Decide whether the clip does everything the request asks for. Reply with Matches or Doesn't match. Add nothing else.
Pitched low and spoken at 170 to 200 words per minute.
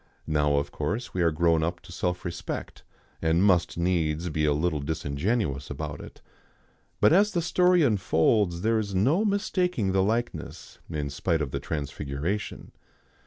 Doesn't match